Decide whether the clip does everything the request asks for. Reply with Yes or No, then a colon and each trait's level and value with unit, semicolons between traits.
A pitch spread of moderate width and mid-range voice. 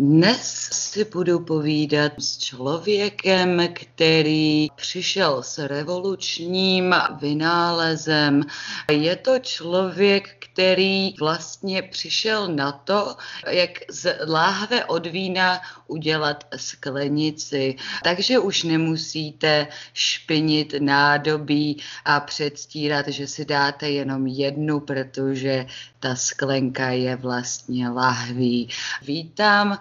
Yes: average, 4.3 semitones; medium, 155 Hz